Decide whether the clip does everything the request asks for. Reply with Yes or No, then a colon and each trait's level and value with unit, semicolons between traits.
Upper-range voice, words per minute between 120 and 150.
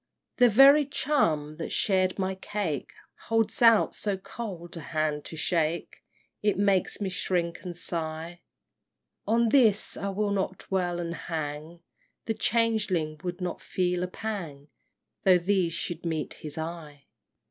No: medium, 180 Hz; average, 145 wpm